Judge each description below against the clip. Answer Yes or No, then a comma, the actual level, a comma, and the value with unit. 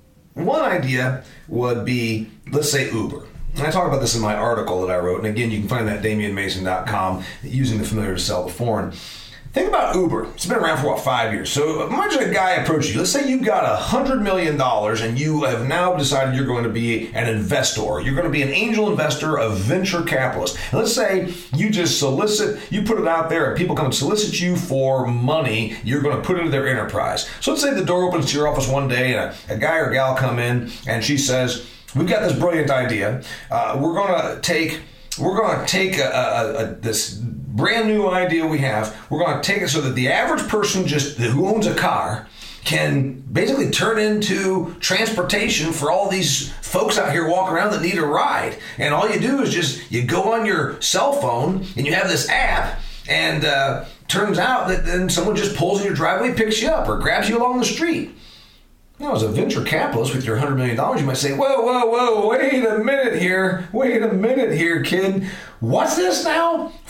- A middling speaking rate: No, fast, 220 wpm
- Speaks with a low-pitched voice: No, medium, 145 Hz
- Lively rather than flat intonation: Yes, wide, 7.7 semitones